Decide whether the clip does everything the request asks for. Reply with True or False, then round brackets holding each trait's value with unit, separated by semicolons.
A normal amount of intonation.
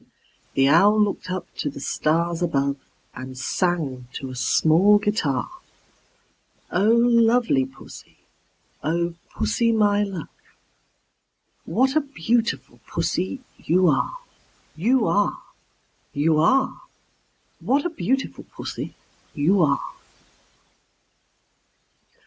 False (7.6 semitones)